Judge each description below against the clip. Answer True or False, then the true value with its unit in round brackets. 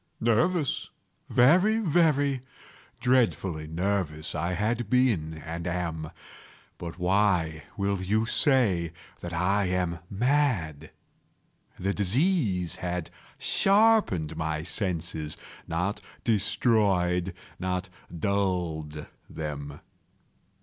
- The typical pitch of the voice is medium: False (95 Hz)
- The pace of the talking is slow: True (80 wpm)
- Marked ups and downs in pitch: True (5.8 semitones)